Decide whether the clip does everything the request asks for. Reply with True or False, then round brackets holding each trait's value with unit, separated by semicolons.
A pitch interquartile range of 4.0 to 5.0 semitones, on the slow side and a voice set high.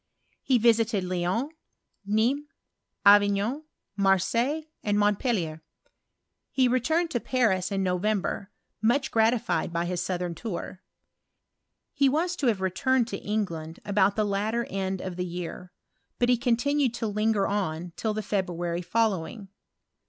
True (4.4 semitones; 130 wpm; 205 Hz)